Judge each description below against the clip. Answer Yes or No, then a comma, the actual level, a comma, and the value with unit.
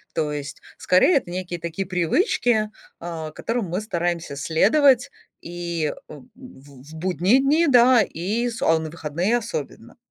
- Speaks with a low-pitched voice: No, medium, 175 Hz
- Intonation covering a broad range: Yes, wide, 6.6 semitones